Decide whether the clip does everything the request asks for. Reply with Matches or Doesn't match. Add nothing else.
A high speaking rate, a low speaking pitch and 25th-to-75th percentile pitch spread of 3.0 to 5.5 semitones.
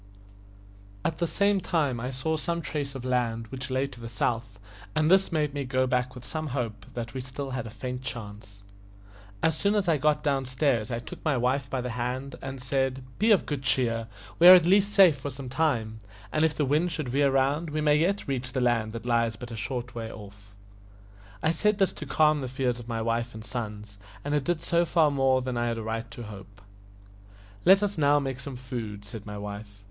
Matches